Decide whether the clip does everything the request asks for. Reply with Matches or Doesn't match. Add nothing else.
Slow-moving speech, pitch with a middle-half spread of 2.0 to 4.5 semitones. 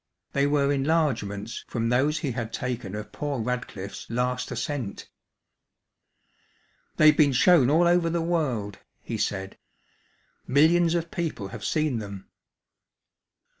Doesn't match